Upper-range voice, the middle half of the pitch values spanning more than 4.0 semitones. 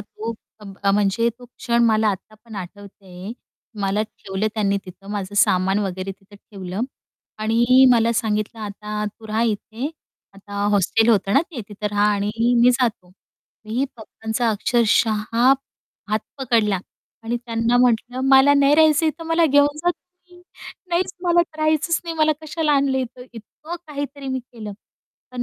Yes: high, 230 Hz; average, 4.8 semitones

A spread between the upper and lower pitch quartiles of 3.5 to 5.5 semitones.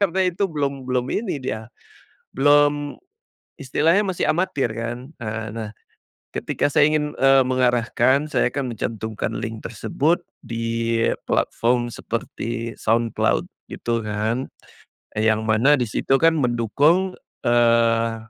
Yes: average, 4.0 semitones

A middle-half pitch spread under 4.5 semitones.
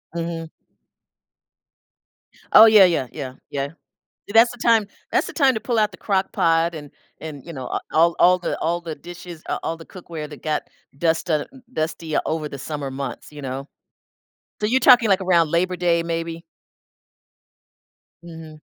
Yes: average, 3.1 semitones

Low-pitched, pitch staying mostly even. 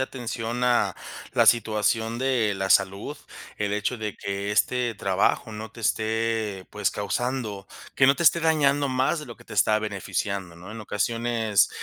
No: low, 110 Hz; average, 3.3 semitones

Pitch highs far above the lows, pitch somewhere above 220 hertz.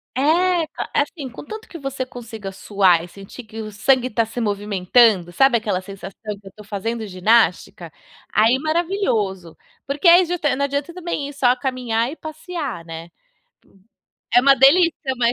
Yes: wide, 5.7 semitones; high, 235 Hz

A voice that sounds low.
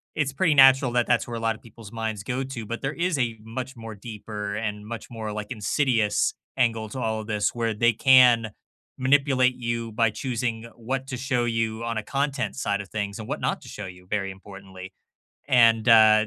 Yes: low, 115 Hz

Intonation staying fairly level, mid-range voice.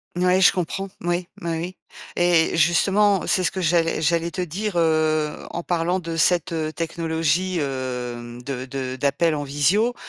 No: average, 3.0 semitones; medium, 165 Hz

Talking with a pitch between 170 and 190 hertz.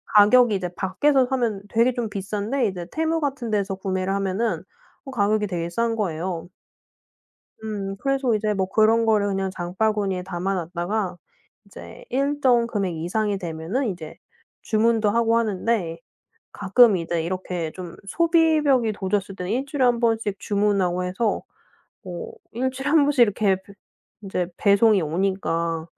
No: high, 205 Hz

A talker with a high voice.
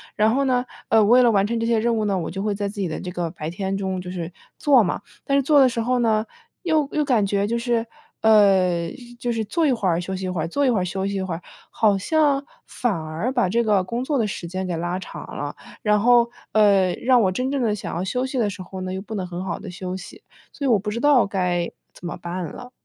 Yes: high, 205 Hz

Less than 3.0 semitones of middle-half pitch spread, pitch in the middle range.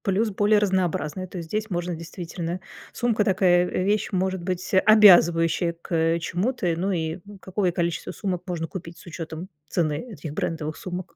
Yes: narrow, 2.5 semitones; medium, 180 Hz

